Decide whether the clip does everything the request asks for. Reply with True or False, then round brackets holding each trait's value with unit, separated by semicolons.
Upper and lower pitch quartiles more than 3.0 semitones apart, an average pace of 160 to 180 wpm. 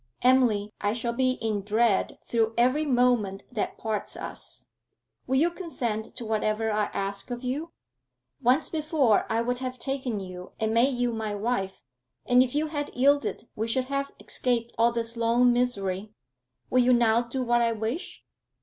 False (2.7 semitones; 170 wpm)